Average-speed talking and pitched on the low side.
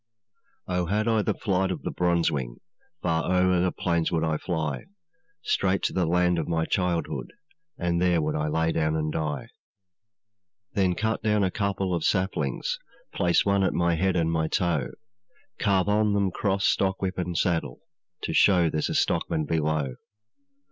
Yes: average, 170 wpm; very low, 90 Hz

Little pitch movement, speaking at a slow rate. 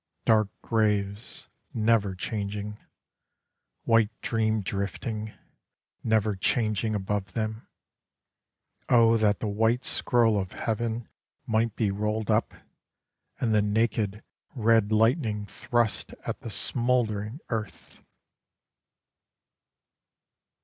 Yes: narrow, 1.7 semitones; slow, 95 wpm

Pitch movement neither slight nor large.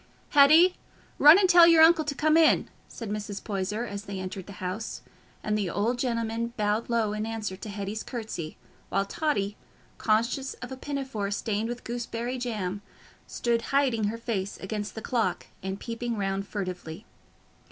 Yes: average, 3.6 semitones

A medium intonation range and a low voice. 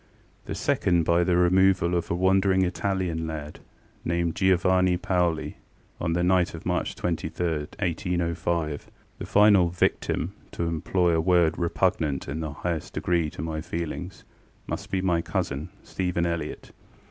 No: narrow, 2.0 semitones; very low, 85 Hz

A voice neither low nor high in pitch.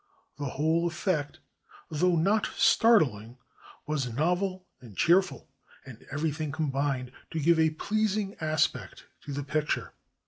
Yes: medium, 155 Hz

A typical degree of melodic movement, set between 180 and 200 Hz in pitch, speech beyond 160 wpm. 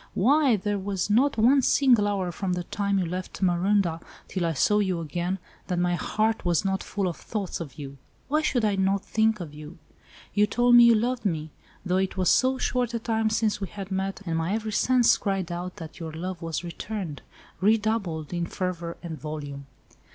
Yes: average, 4.1 semitones; high, 190 Hz; average, 195 wpm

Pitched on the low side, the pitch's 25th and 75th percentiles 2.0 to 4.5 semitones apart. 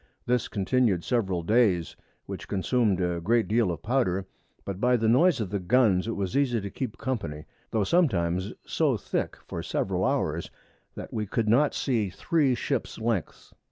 No: low, 110 Hz; average, 4.9 semitones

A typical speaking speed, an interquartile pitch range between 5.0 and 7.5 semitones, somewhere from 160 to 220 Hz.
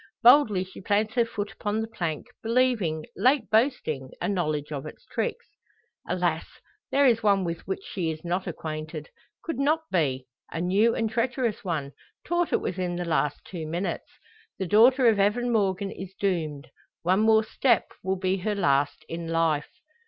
Yes: average, 170 wpm; average, 5.3 semitones; high, 190 Hz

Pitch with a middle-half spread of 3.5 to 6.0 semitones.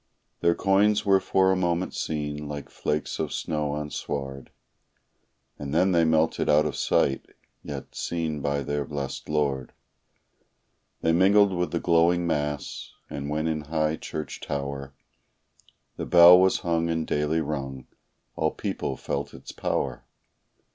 No: average, 2.8 semitones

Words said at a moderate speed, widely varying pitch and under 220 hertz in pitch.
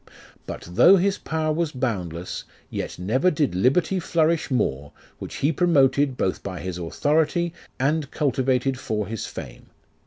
Yes: average, 145 wpm; wide, 7.5 semitones; low, 135 Hz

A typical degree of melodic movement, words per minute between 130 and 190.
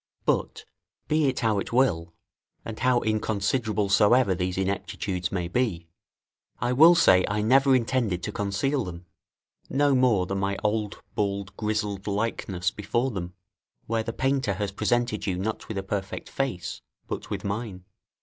Yes: average, 3.9 semitones; average, 155 wpm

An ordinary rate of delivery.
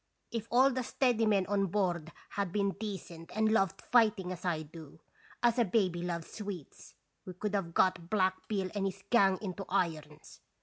Yes: average, 180 wpm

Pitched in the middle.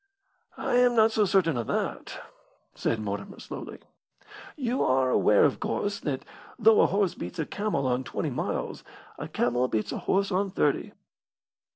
Yes: medium, 165 Hz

